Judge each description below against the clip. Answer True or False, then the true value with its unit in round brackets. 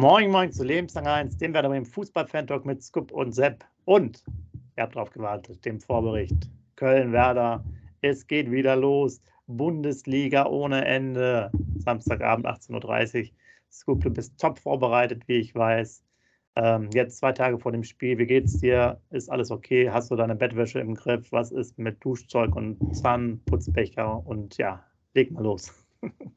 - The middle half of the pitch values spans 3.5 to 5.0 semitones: False (3.1 semitones)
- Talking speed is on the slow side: False (160 wpm)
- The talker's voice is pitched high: False (120 Hz)